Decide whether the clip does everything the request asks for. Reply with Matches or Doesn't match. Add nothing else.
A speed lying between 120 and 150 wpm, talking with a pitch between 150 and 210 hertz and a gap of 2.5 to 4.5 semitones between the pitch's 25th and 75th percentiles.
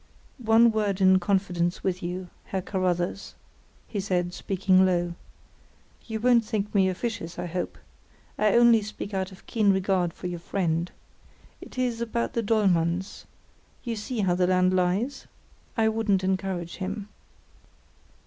Matches